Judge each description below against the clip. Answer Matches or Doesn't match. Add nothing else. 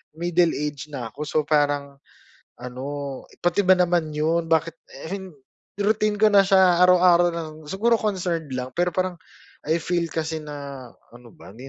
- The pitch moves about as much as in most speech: Matches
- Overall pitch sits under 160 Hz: Doesn't match